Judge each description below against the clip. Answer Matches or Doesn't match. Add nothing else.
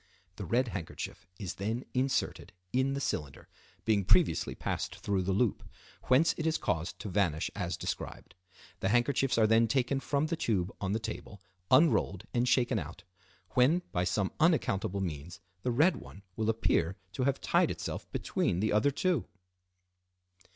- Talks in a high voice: Doesn't match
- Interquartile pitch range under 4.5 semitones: Doesn't match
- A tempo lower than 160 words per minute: Doesn't match